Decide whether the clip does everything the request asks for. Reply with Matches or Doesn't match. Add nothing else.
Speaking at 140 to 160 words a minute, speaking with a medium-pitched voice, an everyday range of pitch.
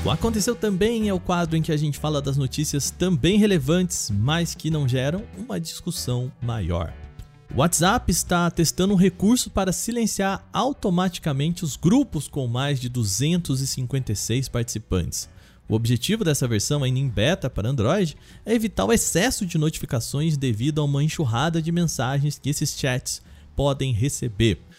Doesn't match